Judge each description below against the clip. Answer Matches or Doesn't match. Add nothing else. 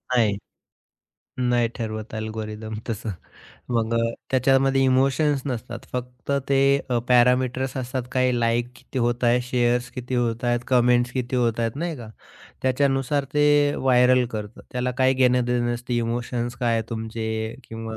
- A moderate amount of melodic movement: Doesn't match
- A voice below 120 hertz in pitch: Doesn't match